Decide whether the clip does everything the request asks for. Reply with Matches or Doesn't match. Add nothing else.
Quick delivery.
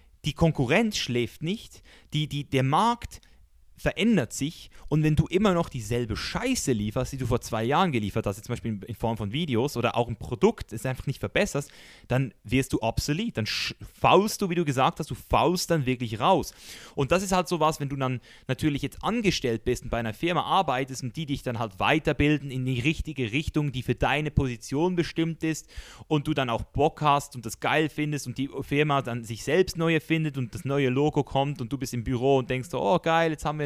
Matches